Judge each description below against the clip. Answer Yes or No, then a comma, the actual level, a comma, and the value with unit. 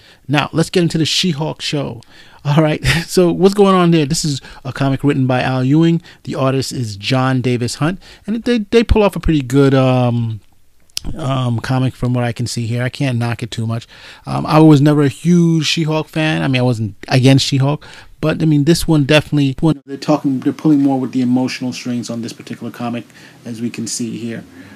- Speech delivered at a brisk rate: Yes, fast, 215 wpm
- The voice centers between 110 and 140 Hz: Yes, low, 135 Hz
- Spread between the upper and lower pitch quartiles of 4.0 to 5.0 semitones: Yes, average, 4.3 semitones